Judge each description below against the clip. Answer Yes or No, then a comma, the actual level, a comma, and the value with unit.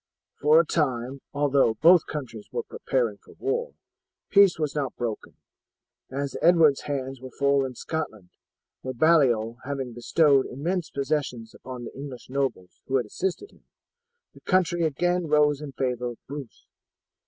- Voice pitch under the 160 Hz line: Yes, medium, 140 Hz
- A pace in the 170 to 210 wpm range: No, average, 150 wpm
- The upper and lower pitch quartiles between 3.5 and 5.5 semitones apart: Yes, average, 4.0 semitones